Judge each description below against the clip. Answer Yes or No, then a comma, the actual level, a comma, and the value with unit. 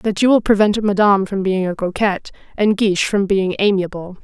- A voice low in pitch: No, high, 200 Hz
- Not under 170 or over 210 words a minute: Yes, average, 200 wpm